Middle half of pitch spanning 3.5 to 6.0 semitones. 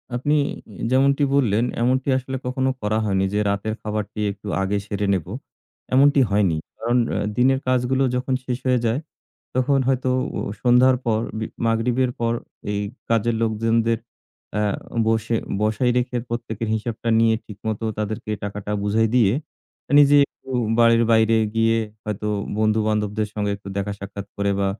No: average, 3.0 semitones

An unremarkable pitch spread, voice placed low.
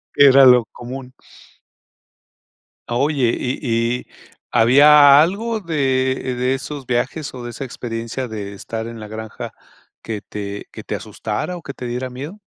Yes: average, 3.3 semitones; low, 125 Hz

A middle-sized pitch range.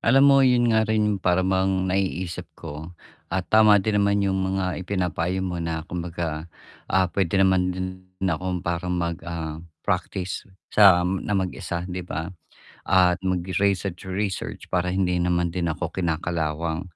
No: narrow, 1.8 semitones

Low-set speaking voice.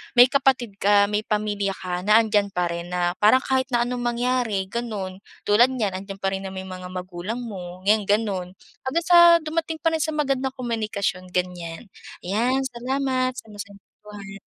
No: high, 210 Hz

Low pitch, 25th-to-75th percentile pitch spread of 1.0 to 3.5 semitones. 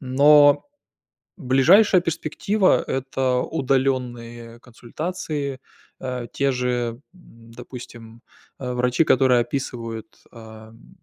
Yes: low, 125 Hz; average, 2.8 semitones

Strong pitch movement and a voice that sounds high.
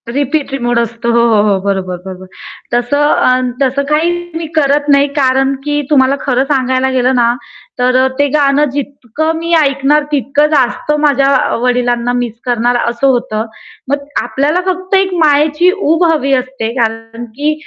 No: average, 3.3 semitones; very high, 270 Hz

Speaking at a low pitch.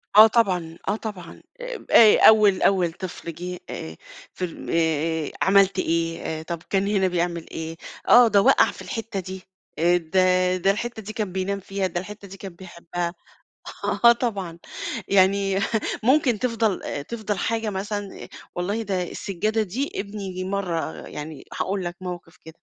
No: high, 190 Hz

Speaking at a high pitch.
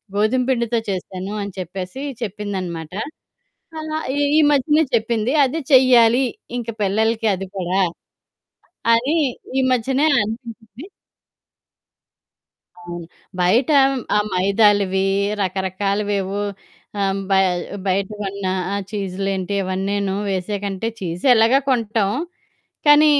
Yes: high, 205 Hz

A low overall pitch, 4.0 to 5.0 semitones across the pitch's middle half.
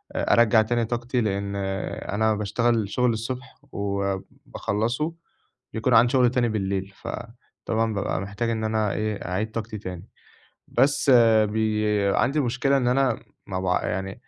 No: low, 110 Hz; average, 3.1 semitones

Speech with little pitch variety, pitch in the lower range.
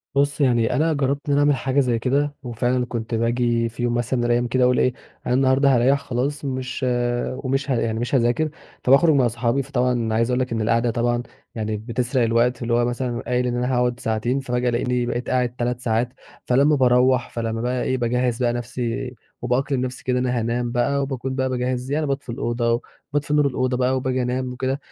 Yes: narrow, 1.7 semitones; low, 125 Hz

